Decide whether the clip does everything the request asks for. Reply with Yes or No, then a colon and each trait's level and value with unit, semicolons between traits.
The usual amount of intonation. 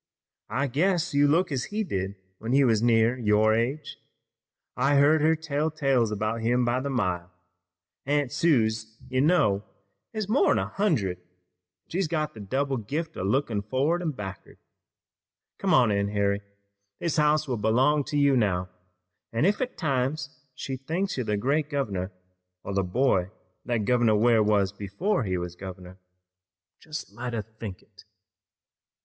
No: wide, 6.2 semitones